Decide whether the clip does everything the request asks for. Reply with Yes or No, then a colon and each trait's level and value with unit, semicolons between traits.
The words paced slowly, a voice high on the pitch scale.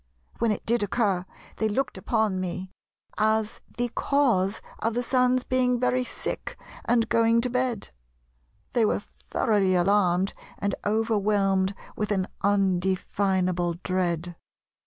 Yes: slow, 125 wpm; high, 205 Hz